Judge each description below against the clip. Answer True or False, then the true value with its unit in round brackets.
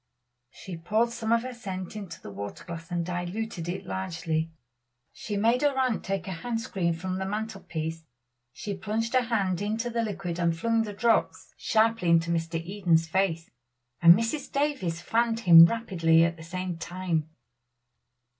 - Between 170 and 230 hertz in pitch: True (190 Hz)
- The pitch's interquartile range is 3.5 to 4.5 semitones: False (5.1 semitones)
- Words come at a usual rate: True (170 wpm)